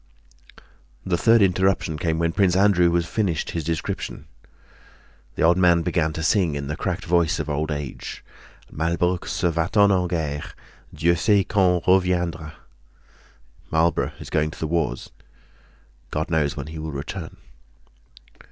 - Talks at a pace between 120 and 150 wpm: Yes, average, 145 wpm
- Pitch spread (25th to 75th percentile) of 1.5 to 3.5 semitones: Yes, narrow, 2.5 semitones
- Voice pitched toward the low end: Yes, very low, 85 Hz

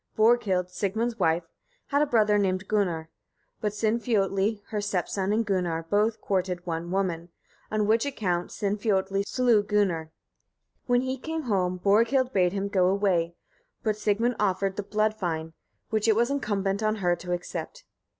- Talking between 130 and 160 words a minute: Yes, average, 155 wpm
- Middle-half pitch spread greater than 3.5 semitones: No, average, 3.2 semitones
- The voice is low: No, high, 205 Hz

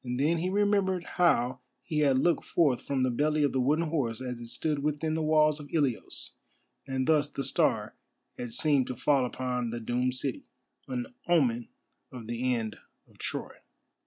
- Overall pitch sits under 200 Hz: Yes, low, 135 Hz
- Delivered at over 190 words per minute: No, average, 180 wpm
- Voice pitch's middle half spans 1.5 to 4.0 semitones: Yes, average, 3.7 semitones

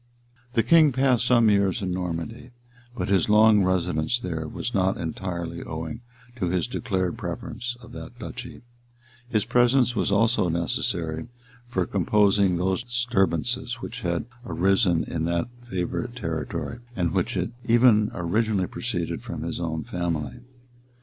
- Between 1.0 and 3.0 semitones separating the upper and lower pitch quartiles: No, wide, 5.5 semitones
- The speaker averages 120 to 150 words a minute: Yes, average, 140 wpm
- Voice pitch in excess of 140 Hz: No, very low, 95 Hz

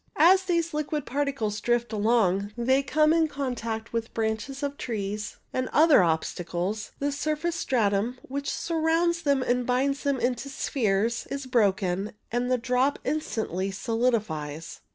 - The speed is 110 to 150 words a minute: Yes, average, 140 wpm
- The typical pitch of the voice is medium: No, very high, 250 Hz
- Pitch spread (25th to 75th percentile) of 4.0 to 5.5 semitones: Yes, average, 4.9 semitones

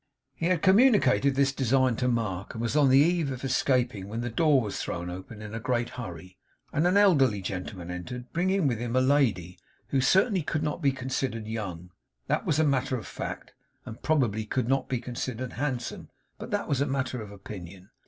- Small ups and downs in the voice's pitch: No, average, 4.6 semitones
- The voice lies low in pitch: Yes, low, 125 Hz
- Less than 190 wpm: No, average, 195 wpm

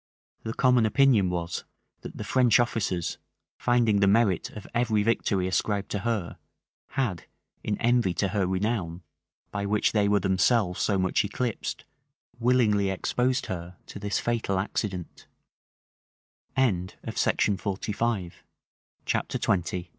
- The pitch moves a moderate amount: Yes, average, 3.8 semitones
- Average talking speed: No, slow, 115 wpm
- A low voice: Yes, low, 105 Hz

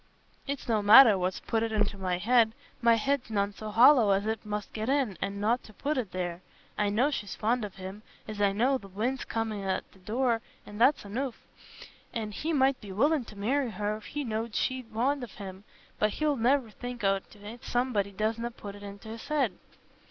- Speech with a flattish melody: No, average, 3.6 semitones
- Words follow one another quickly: Yes, fast, 210 wpm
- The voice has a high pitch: Yes, high, 220 Hz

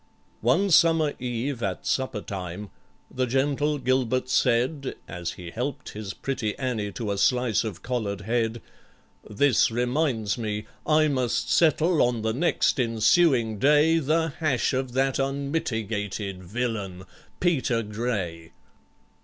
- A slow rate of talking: Yes, slow, 130 wpm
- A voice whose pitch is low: Yes, low, 125 Hz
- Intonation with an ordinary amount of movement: Yes, average, 4.7 semitones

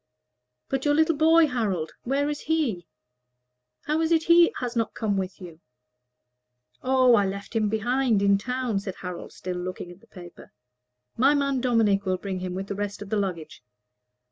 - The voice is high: Yes, high, 215 Hz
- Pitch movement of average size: No, wide, 6.1 semitones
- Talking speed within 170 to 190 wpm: Yes, average, 180 wpm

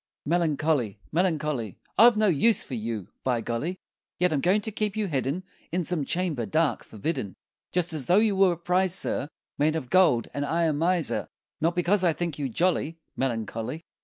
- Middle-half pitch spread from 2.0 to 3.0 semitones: No, average, 5.2 semitones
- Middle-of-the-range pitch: Yes, medium, 160 Hz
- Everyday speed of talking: Yes, average, 185 wpm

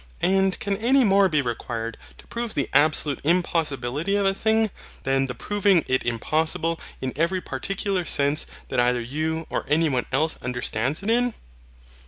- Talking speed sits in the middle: Yes, average, 165 wpm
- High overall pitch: No, medium, 160 Hz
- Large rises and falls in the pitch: Yes, wide, 6.7 semitones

